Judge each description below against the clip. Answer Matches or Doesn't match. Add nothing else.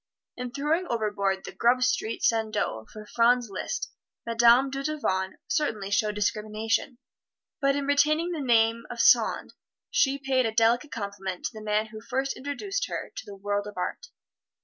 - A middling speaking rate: Matches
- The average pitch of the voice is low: Doesn't match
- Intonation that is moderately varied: Matches